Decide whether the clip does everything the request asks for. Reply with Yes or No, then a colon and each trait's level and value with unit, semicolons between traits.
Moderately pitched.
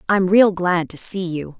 Yes: medium, 180 Hz